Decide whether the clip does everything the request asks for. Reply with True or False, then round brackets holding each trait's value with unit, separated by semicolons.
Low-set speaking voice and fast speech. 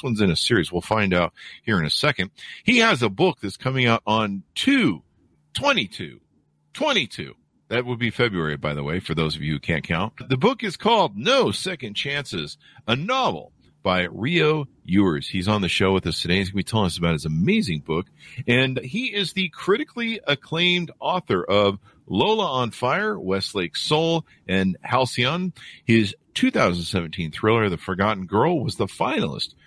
False (115 Hz; 175 wpm)